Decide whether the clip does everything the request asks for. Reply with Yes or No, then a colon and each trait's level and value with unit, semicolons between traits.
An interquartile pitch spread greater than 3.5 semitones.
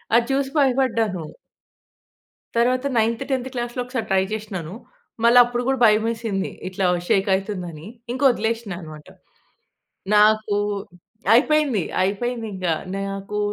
Yes: average, 3.9 semitones